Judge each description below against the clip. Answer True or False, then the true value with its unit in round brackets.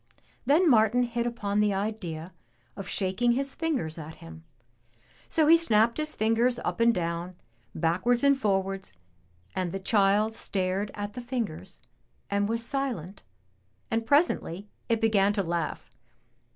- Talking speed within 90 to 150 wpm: True (140 wpm)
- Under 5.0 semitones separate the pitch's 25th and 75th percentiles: True (4.2 semitones)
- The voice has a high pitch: True (210 Hz)